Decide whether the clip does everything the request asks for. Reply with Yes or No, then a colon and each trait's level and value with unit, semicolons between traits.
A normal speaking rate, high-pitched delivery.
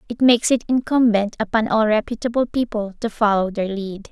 Yes: average, 175 wpm; high, 220 Hz